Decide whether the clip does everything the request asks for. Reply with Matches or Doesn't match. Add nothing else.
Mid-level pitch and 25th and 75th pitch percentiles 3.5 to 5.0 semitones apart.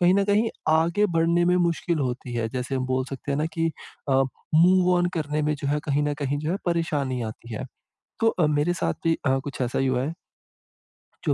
Matches